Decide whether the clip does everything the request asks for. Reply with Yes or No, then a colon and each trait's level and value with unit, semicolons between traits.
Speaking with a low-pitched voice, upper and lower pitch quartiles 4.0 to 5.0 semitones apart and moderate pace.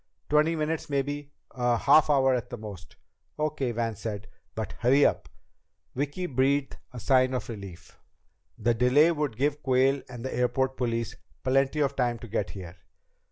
No: low, 130 Hz; average, 3.4 semitones; average, 170 wpm